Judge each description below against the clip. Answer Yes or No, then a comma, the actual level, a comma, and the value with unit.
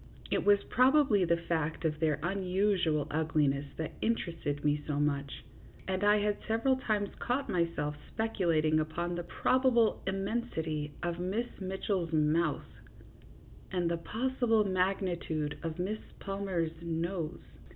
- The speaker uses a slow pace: Yes, slow, 130 wpm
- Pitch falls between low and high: Yes, medium, 175 Hz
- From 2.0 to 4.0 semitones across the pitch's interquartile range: No, average, 4.6 semitones